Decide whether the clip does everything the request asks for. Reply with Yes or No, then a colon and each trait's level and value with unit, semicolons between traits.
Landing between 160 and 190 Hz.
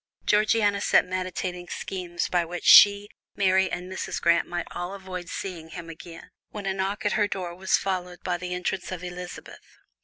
Yes: medium, 185 Hz